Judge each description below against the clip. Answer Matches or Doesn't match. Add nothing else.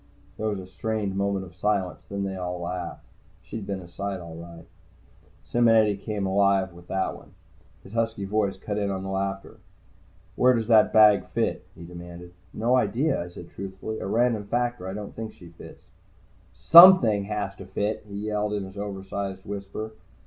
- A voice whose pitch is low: Matches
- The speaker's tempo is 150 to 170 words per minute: Doesn't match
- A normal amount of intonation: Doesn't match